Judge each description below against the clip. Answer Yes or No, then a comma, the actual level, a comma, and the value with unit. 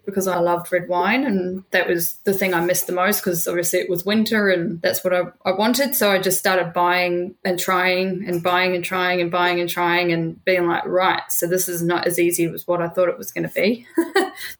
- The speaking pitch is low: No, medium, 180 Hz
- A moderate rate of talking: No, fast, 245 wpm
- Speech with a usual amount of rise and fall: No, narrow, 1.3 semitones